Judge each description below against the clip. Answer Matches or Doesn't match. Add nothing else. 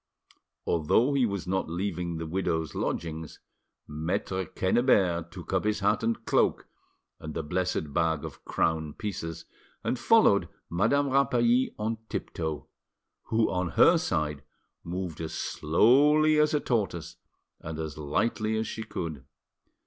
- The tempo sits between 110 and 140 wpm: Matches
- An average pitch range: Doesn't match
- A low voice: Matches